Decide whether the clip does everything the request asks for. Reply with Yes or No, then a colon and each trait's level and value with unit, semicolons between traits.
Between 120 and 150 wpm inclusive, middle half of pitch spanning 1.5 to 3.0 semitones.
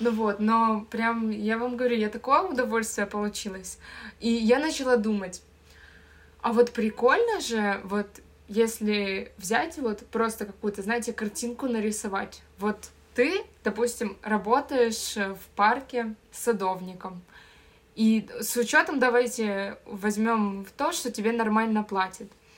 Yes: average, 125 wpm; narrow, 2.5 semitones